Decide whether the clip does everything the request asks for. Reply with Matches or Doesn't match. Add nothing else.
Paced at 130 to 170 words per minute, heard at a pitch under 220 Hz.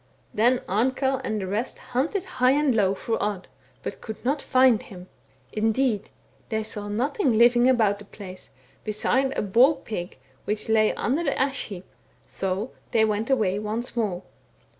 Doesn't match